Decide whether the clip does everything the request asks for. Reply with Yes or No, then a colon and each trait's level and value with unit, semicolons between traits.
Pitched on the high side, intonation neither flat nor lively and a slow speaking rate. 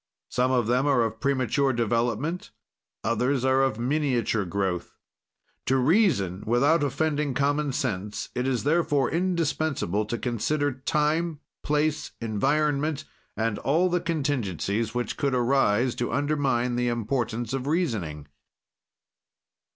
No: low, 130 Hz; average, 4.2 semitones; slow, 120 wpm